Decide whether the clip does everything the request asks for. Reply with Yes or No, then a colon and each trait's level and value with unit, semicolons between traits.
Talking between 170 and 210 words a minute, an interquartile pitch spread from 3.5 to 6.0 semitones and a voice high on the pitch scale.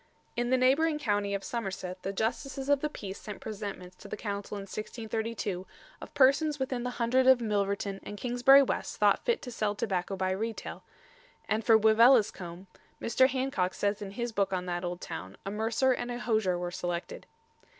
Yes: average, 185 wpm; average, 4.3 semitones; high, 220 Hz